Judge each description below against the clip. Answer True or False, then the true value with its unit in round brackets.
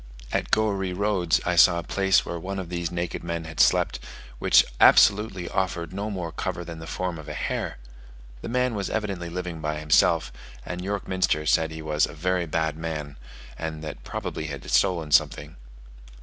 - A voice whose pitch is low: True (85 Hz)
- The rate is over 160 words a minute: True (185 wpm)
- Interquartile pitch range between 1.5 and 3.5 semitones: True (2.9 semitones)